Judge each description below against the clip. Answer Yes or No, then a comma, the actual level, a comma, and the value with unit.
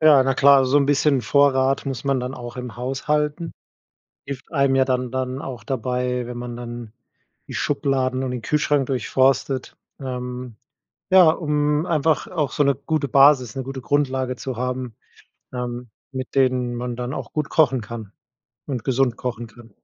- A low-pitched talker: Yes, low, 130 Hz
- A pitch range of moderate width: No, narrow, 2.1 semitones